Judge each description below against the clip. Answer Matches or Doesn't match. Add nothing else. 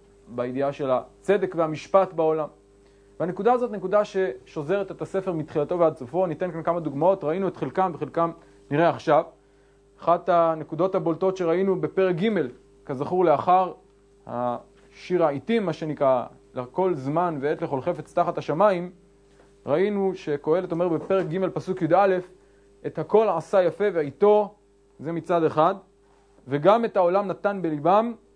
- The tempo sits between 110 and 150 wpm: Matches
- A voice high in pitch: Doesn't match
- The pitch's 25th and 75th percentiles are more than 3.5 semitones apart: Matches